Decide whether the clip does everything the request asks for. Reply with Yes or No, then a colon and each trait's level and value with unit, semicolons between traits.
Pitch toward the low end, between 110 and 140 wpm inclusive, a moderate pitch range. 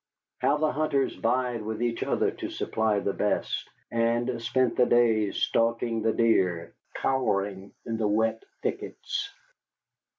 No: low, 115 Hz; slow, 135 wpm; narrow, 2.3 semitones